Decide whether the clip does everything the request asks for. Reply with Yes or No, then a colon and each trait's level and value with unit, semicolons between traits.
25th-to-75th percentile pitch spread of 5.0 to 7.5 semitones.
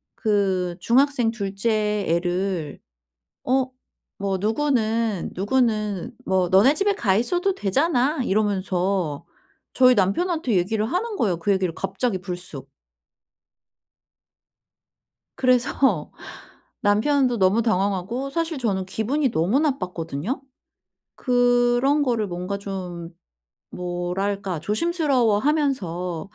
Yes: wide, 5.6 semitones